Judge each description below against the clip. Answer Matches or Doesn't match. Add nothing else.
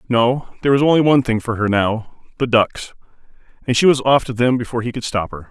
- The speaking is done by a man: Matches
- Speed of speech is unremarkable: Doesn't match